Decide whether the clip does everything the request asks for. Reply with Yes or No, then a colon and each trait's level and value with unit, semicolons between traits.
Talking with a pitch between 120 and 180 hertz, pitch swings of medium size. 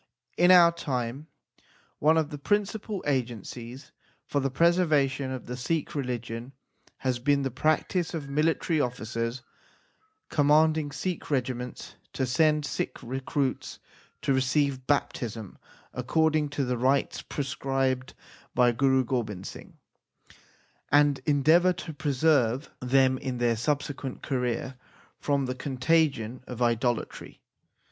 Yes: low, 135 Hz; average, 3.3 semitones